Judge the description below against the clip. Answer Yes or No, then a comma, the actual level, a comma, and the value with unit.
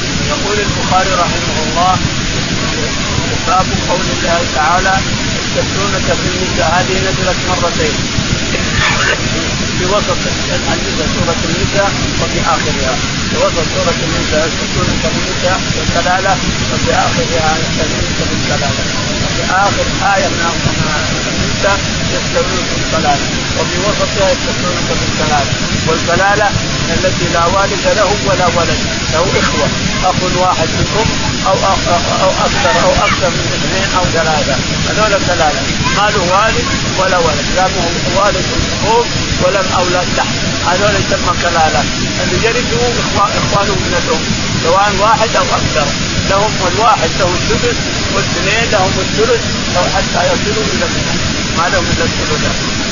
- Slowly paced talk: No, average, 120 wpm